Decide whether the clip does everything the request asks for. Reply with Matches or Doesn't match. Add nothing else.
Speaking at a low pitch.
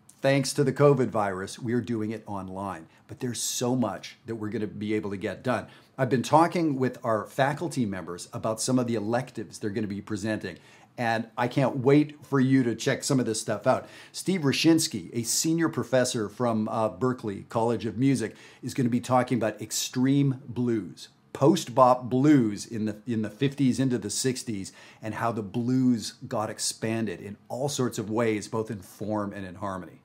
Matches